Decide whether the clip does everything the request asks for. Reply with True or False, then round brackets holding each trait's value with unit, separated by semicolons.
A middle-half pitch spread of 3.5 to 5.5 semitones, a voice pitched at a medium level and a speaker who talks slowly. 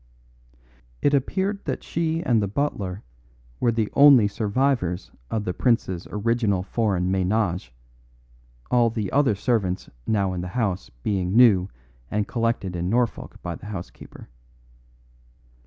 False (4.6 semitones; 105 Hz; 125 wpm)